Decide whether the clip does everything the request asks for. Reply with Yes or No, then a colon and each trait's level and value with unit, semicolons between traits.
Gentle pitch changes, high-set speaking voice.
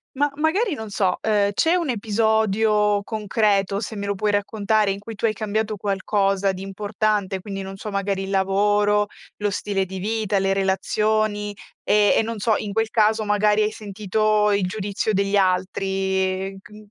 Yes: narrow, 1.8 semitones; high, 205 Hz